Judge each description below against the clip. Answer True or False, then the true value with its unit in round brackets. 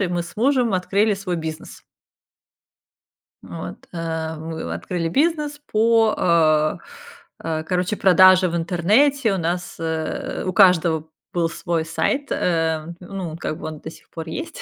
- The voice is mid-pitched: True (175 Hz)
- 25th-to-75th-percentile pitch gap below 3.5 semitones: False (3.9 semitones)